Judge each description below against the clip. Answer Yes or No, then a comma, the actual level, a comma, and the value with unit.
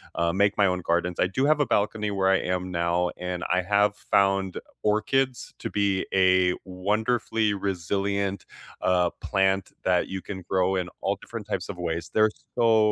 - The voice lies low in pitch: Yes, very low, 95 Hz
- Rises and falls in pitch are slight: Yes, narrow, 2.2 semitones